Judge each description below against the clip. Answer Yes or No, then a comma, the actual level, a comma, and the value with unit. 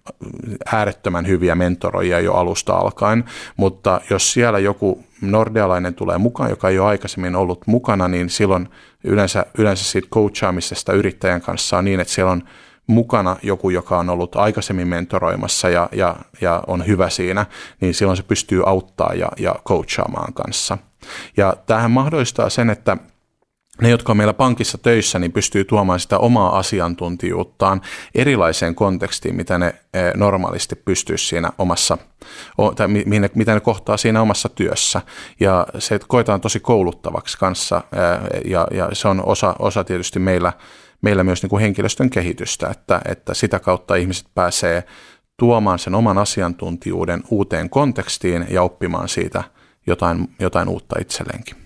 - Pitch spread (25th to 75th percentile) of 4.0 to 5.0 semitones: No, average, 3.2 semitones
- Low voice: Yes, very low, 95 Hz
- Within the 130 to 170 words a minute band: Yes, average, 145 wpm